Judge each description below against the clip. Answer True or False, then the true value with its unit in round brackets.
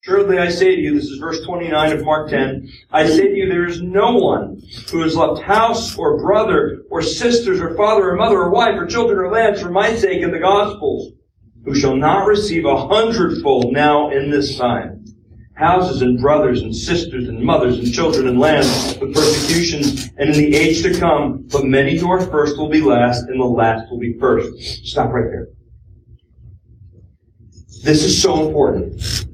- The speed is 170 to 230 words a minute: True (190 wpm)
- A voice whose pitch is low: False (150 Hz)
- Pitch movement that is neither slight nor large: False (6.9 semitones)